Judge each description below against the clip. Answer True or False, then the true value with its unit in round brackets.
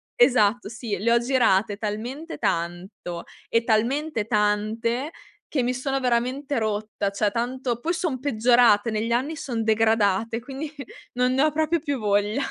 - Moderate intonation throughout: True (3.7 semitones)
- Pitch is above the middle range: True (235 Hz)